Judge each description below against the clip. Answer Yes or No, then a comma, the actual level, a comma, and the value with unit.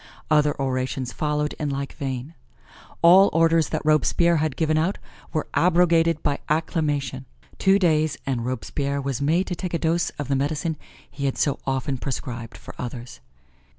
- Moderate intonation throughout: Yes, average, 3.4 semitones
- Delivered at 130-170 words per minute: Yes, average, 160 wpm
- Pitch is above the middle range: No, medium, 150 Hz